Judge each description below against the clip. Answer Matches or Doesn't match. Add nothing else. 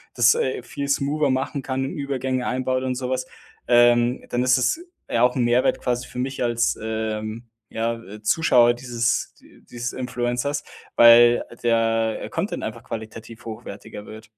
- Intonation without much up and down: Matches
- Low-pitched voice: Matches